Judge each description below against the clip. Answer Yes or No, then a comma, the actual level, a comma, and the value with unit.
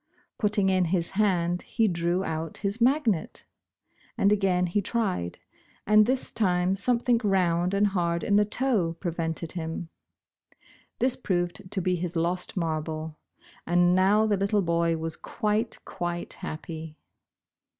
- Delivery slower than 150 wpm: Yes, average, 140 wpm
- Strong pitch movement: No, average, 3.6 semitones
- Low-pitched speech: No, medium, 180 Hz